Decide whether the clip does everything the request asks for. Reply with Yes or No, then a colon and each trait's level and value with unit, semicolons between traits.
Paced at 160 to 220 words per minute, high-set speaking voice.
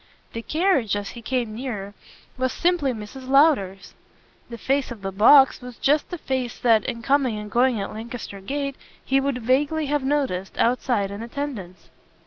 Yes: average, 170 wpm; very high, 250 Hz